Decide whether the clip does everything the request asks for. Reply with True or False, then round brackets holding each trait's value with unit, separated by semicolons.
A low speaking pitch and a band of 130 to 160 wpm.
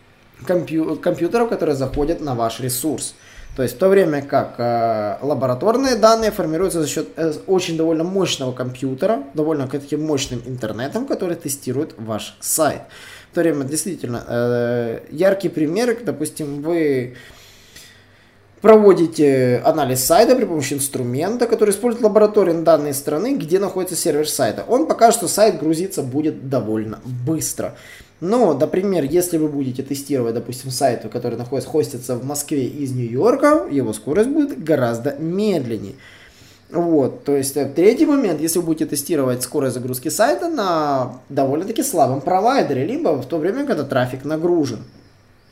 False (150 Hz; 140 wpm)